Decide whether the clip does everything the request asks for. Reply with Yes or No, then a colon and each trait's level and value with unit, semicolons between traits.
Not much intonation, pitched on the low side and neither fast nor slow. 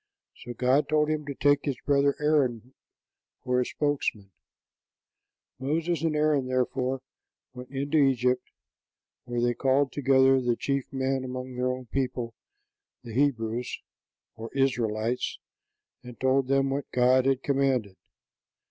No: narrow, 2.0 semitones; low, 130 Hz; slow, 130 wpm